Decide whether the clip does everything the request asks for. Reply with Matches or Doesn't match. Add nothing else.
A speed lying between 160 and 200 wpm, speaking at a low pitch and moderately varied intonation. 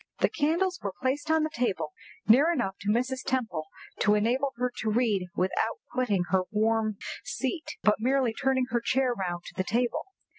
Doesn't match